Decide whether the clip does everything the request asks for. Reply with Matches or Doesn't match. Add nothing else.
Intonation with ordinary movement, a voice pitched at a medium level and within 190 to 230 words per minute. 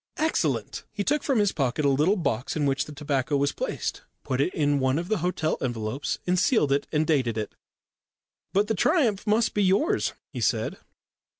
Doesn't match